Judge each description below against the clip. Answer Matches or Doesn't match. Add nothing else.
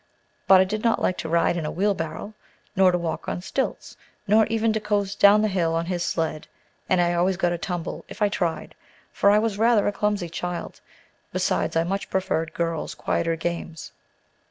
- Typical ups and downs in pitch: Matches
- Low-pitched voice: Doesn't match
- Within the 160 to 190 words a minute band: Doesn't match